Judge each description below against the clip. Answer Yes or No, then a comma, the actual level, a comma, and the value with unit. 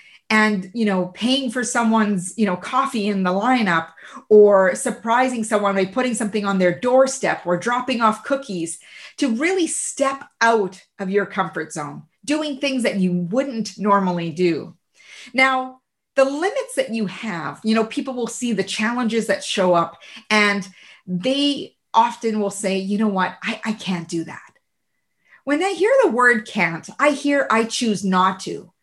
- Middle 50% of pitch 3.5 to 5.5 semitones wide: Yes, average, 5.2 semitones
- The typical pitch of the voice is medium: No, high, 220 Hz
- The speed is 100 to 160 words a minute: No, average, 170 wpm